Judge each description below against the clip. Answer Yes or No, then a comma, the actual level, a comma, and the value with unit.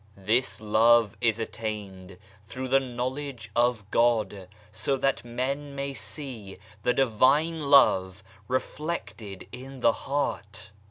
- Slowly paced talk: Yes, slow, 110 wpm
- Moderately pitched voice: No, low, 120 Hz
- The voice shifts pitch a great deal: No, average, 4.2 semitones